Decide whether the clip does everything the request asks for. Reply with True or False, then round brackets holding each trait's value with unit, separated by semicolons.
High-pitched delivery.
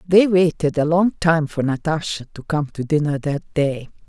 False (155 Hz)